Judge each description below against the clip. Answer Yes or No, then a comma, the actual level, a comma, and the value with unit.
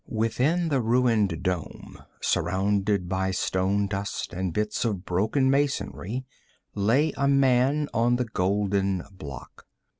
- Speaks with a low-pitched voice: Yes, low, 105 Hz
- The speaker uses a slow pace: Yes, slow, 120 wpm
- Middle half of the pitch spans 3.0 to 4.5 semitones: No, average, 5.1 semitones